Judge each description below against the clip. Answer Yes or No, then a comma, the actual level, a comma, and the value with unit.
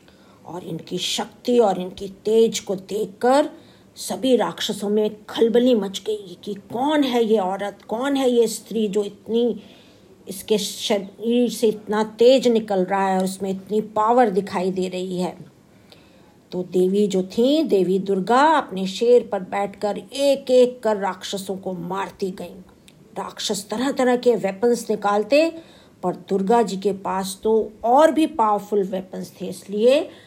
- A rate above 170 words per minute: No, average, 150 wpm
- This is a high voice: Yes, high, 210 Hz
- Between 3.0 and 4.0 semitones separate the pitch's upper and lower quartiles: Yes, average, 3.6 semitones